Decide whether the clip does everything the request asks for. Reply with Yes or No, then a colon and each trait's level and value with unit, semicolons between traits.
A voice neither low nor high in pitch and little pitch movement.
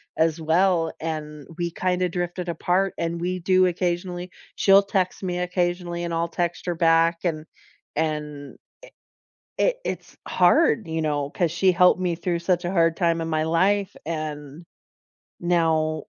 Yes: medium, 170 Hz; narrow, 2.0 semitones